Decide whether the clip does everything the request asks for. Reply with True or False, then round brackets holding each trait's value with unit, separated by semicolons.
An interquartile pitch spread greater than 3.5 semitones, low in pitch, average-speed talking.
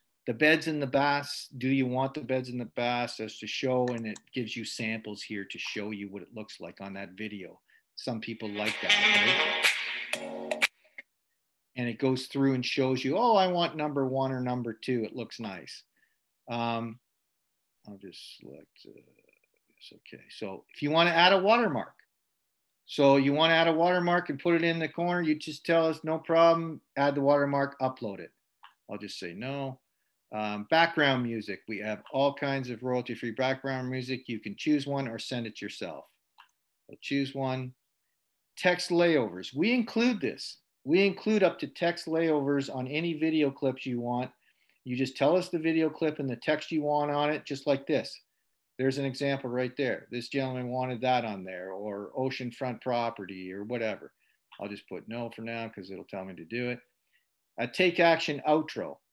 True (4.7 semitones; 130 Hz; 190 wpm)